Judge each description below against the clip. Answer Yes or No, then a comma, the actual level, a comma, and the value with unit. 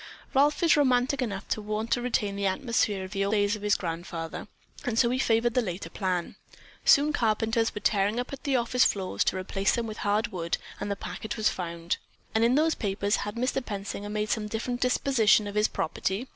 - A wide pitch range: No, average, 3.6 semitones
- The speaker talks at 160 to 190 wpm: No, fast, 205 wpm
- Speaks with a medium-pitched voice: No, high, 215 Hz